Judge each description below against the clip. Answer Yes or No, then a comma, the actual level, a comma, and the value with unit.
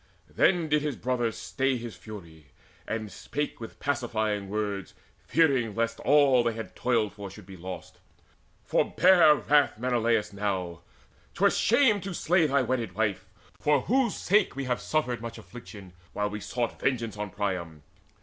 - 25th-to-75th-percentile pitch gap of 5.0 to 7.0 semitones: Yes, wide, 5.5 semitones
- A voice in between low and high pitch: No, low, 115 Hz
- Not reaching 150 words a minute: No, average, 155 wpm